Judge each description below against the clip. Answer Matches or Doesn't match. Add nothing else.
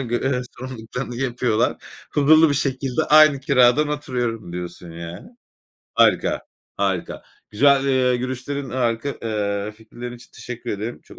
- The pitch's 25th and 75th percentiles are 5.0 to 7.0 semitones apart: Doesn't match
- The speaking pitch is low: Matches